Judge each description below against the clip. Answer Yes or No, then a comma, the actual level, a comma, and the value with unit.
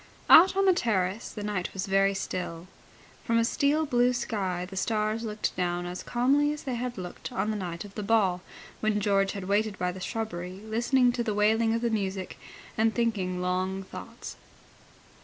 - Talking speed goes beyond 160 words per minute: Yes, average, 190 wpm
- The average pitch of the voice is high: Yes, high, 210 Hz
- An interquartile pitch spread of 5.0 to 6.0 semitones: No, average, 3.7 semitones